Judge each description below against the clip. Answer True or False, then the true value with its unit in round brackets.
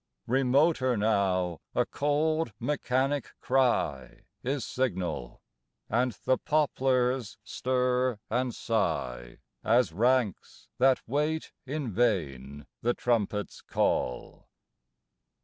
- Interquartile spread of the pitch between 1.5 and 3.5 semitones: False (4.6 semitones)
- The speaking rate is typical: False (95 wpm)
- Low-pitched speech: True (125 Hz)